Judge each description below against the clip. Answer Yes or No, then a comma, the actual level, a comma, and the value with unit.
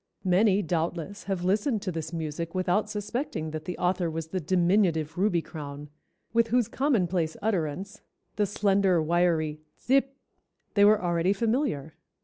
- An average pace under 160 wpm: Yes, average, 140 wpm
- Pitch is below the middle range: No, medium, 185 Hz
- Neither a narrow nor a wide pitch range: Yes, average, 4.2 semitones